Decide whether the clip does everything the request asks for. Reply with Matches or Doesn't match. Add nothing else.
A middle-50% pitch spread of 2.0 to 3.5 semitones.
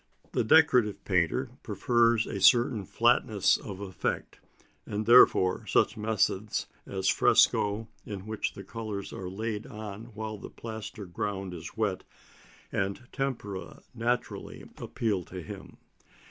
Matches